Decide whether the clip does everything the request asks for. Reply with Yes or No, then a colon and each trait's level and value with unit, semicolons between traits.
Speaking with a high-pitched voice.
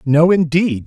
No: medium, 160 Hz